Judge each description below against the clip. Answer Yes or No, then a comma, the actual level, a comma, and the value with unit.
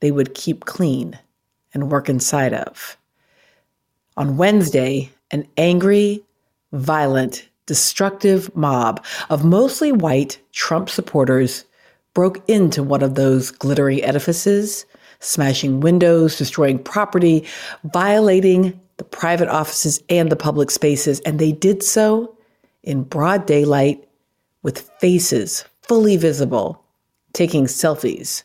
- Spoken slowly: Yes, slow, 110 wpm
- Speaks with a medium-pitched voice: Yes, medium, 155 Hz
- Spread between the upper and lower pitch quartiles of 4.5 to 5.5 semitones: Yes, average, 5.1 semitones